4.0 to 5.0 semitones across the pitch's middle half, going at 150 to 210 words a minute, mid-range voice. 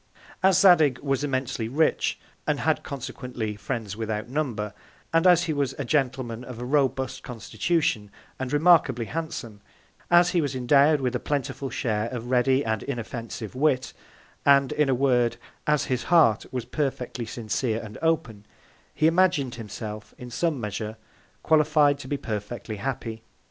No: average, 4.3 semitones; average, 155 wpm; low, 130 Hz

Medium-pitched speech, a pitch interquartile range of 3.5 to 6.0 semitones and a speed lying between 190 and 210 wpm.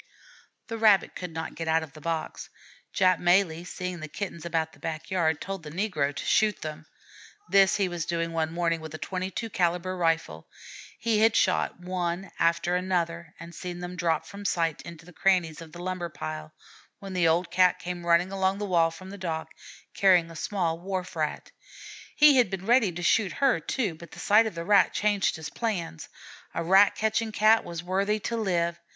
No: medium, 175 Hz; average, 2.9 semitones; average, 200 wpm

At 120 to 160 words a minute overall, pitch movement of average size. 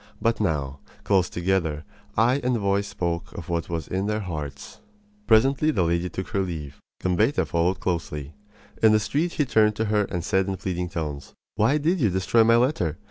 No: average, 190 wpm; average, 4.7 semitones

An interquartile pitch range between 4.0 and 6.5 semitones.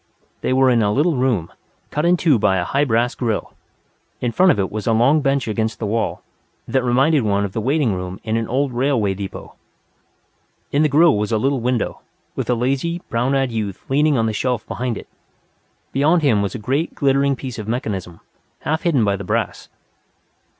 Yes: average, 4.4 semitones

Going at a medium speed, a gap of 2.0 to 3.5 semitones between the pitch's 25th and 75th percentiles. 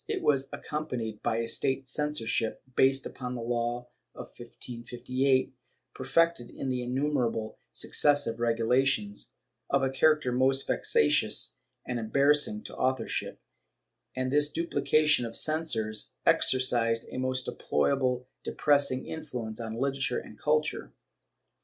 No: slow, 115 wpm; average, 3.1 semitones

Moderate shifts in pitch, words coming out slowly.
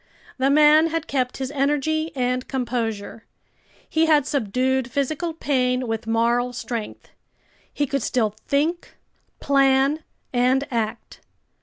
Yes: average, 3.2 semitones; slow, 120 wpm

